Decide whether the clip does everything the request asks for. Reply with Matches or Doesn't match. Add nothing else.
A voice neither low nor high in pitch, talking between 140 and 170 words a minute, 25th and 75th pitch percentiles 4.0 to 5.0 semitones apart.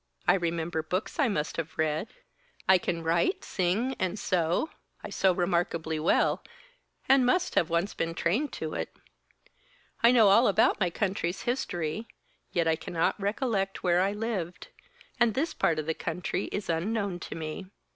Matches